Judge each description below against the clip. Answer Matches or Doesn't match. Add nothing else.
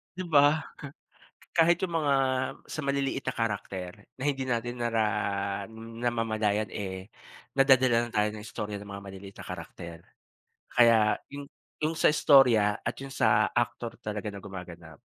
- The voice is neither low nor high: Doesn't match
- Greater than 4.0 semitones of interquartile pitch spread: Matches